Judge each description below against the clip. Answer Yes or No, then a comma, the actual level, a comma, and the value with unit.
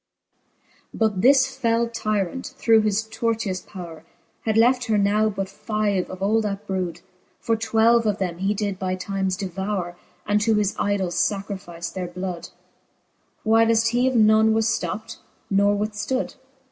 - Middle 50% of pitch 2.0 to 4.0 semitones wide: Yes, average, 2.7 semitones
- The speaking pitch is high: Yes, high, 210 Hz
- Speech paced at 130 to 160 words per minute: Yes, average, 155 wpm